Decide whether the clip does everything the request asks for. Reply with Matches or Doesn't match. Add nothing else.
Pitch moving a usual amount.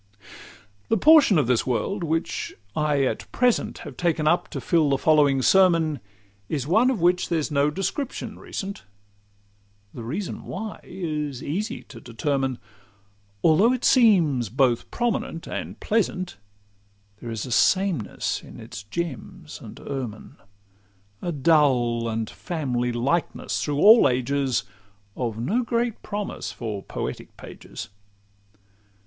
Doesn't match